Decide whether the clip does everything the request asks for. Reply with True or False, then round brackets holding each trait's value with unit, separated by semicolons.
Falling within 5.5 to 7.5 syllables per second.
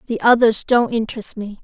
True (5.7 syllables/s)